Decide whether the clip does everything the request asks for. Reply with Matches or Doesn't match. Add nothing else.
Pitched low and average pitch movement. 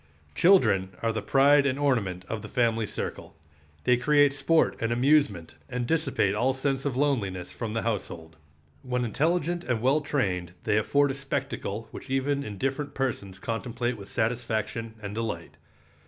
Matches